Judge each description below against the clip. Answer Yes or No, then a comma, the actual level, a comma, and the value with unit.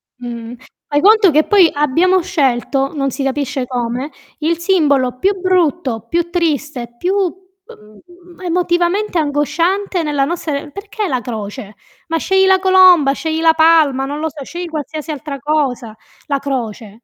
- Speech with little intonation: No, average, 4.6 semitones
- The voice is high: Yes, very high, 305 Hz